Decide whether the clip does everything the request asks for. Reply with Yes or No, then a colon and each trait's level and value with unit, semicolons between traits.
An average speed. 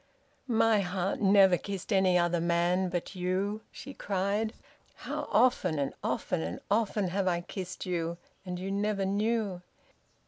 Yes: average, 145 wpm